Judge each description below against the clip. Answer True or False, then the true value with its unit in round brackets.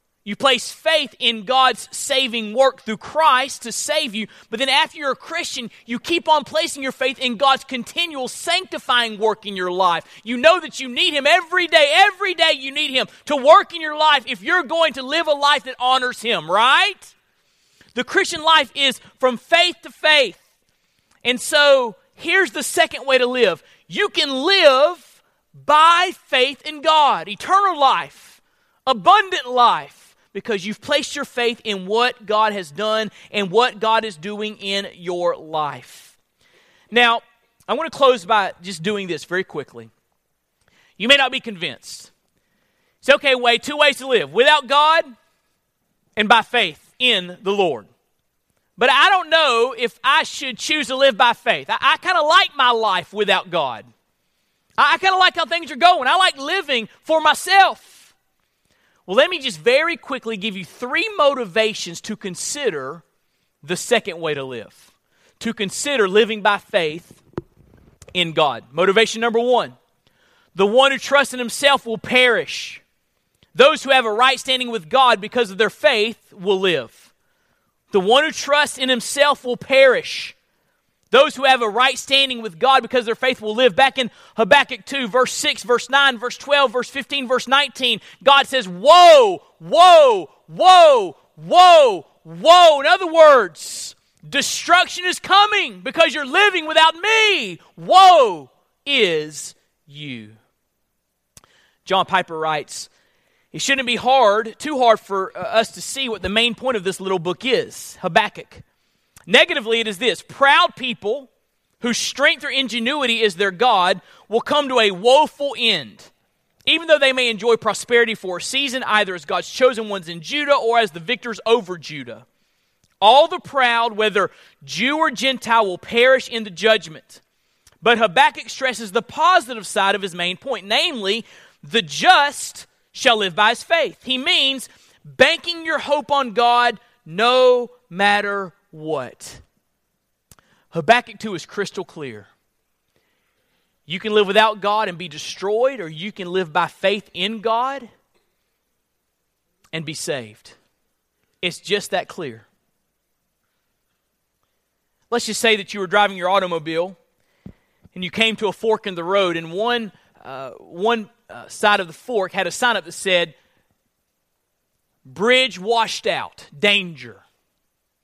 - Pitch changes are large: True (6.2 semitones)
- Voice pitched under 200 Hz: False (245 Hz)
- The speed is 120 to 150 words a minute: False (160 wpm)